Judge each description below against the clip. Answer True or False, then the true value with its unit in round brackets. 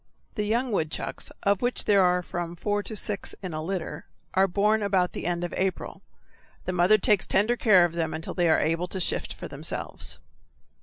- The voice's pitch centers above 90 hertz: True (185 Hz)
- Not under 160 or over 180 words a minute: False (200 wpm)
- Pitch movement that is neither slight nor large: True (3.0 semitones)